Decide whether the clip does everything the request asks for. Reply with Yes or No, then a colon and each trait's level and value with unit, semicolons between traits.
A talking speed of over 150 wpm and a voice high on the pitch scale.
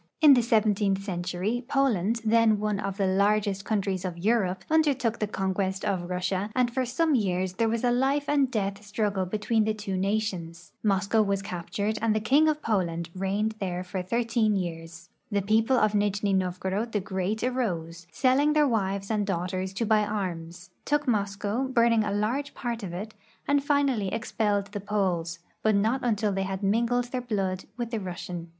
Yes: average, 185 wpm; high, 205 Hz